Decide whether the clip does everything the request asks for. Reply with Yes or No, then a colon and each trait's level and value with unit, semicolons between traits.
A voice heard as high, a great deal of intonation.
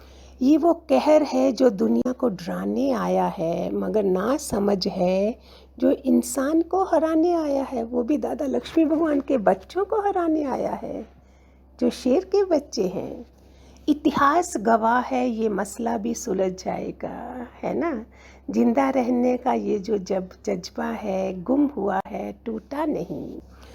Yes: very high, 250 Hz; wide, 6.7 semitones